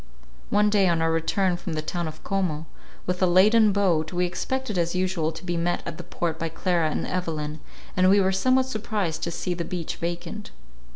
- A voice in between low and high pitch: Yes, medium, 175 Hz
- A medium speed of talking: No, fast, 210 wpm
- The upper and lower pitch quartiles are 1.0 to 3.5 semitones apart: Yes, average, 2.8 semitones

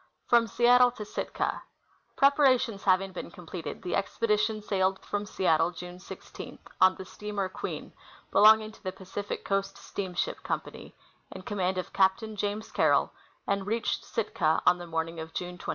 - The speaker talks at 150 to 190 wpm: Yes, average, 155 wpm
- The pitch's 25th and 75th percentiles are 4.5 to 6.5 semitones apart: No, average, 2.8 semitones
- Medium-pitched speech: No, high, 195 Hz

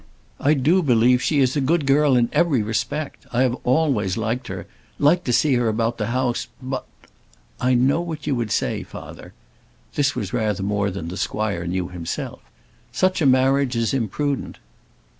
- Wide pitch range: No, average, 4.3 semitones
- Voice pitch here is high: No, low, 125 Hz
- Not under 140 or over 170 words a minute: No, average, 180 wpm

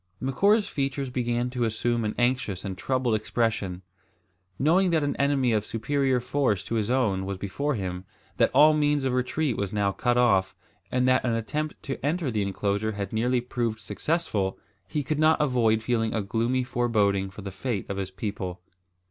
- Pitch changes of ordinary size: Yes, average, 4.7 semitones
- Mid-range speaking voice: No, low, 120 Hz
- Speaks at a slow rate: No, average, 180 wpm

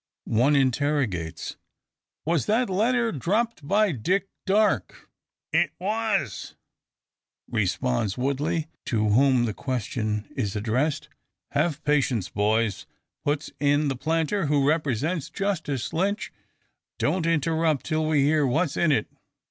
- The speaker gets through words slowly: Yes, slow, 115 wpm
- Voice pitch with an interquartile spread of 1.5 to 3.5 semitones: No, wide, 5.5 semitones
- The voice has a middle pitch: Yes, medium, 145 Hz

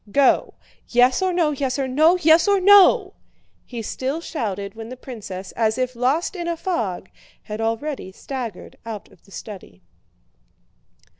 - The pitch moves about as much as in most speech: No, wide, 6.7 semitones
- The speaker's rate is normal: Yes, average, 155 wpm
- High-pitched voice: Yes, very high, 255 Hz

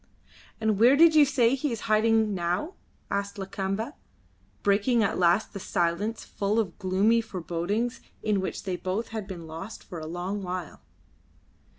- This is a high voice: Yes, high, 205 Hz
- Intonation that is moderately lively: Yes, average, 3.5 semitones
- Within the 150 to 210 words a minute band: Yes, average, 160 wpm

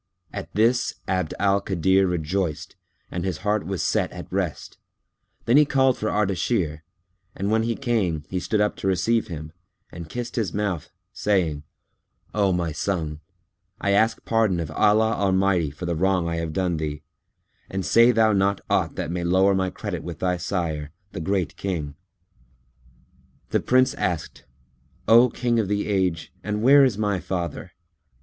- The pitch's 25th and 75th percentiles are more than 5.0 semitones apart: No, average, 3.8 semitones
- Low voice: Yes, very low, 95 Hz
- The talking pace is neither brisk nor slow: Yes, average, 165 wpm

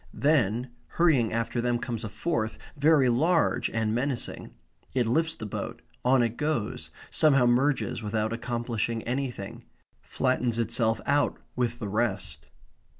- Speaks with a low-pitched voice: Yes, low, 120 Hz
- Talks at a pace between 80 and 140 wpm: Yes, slow, 135 wpm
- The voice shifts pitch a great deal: No, average, 3.4 semitones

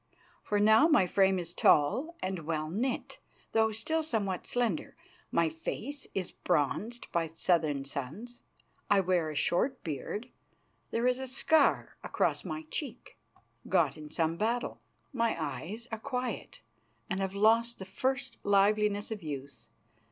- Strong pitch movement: Yes, wide, 6.4 semitones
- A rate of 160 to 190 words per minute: No, average, 145 wpm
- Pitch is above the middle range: Yes, high, 205 Hz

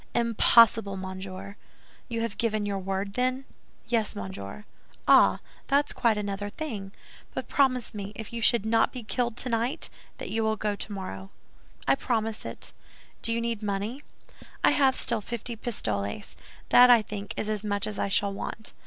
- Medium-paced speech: Yes, average, 165 wpm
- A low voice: No, high, 215 Hz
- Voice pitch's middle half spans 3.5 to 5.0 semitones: No, average, 2.9 semitones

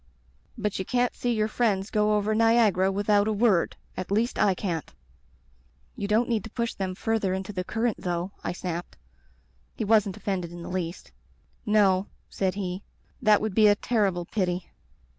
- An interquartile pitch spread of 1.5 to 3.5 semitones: Yes, average, 2.8 semitones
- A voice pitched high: Yes, high, 205 Hz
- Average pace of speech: Yes, average, 175 wpm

